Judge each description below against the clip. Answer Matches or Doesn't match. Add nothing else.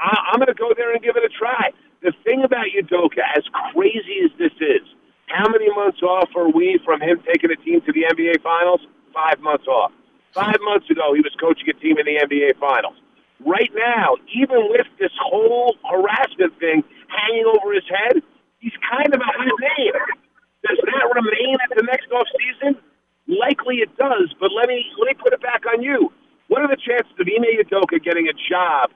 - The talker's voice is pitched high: Matches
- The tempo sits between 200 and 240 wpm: Matches